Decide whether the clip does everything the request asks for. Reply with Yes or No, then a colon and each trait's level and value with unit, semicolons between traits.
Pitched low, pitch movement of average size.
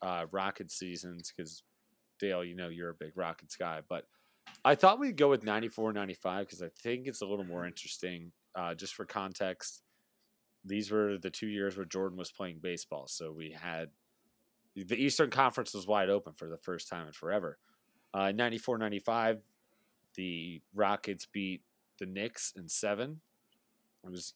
Yes: low, 100 Hz; average, 3.7 semitones